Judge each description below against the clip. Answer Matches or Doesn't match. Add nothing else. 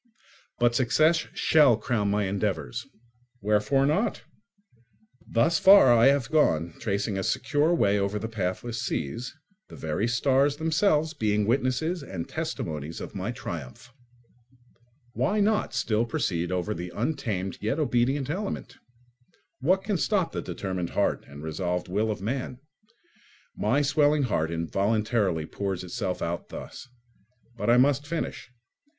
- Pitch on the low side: Matches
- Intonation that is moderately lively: Doesn't match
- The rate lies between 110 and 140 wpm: Matches